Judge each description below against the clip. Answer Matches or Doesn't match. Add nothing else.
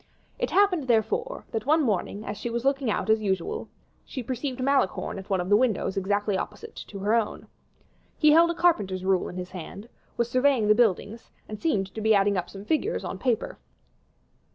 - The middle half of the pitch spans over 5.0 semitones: Matches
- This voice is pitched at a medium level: Doesn't match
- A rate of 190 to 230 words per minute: Matches